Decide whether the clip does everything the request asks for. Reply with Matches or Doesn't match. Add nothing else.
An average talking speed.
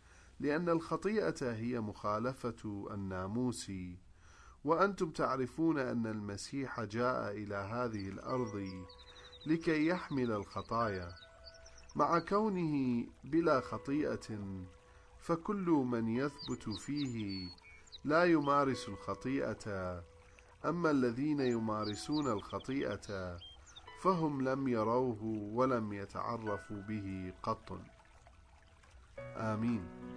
Doesn't match